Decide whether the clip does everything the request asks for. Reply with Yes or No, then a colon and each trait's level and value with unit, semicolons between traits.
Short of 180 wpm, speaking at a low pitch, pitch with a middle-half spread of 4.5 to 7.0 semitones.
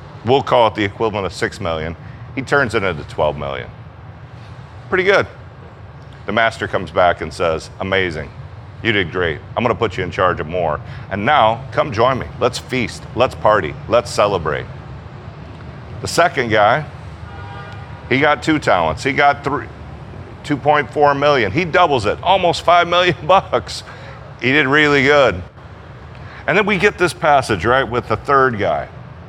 Yes: average, 165 wpm; low, 130 Hz; wide, 5.6 semitones